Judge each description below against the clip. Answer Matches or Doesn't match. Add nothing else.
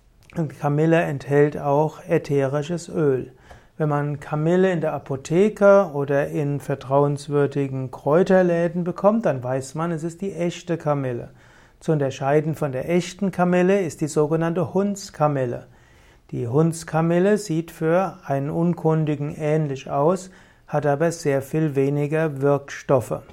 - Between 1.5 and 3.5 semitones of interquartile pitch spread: Matches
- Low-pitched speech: Doesn't match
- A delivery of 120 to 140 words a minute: Matches